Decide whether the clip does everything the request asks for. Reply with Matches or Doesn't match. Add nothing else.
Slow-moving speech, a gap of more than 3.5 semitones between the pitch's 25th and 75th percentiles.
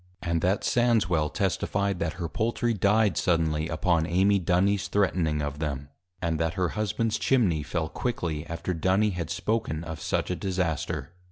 Doesn't match